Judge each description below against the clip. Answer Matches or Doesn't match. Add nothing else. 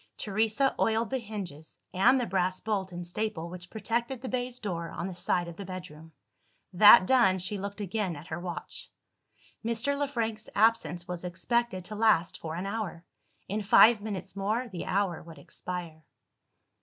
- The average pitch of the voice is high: Matches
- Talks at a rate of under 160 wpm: Doesn't match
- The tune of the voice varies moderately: Matches